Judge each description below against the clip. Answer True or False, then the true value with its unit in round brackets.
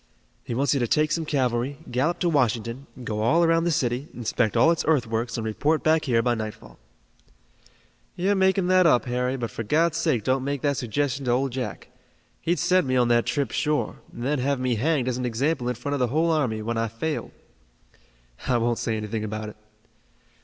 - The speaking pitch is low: True (130 Hz)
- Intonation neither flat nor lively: True (4.5 semitones)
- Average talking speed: False (210 wpm)